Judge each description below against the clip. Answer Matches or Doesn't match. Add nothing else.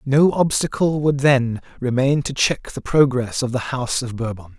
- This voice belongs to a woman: Doesn't match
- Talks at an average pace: Matches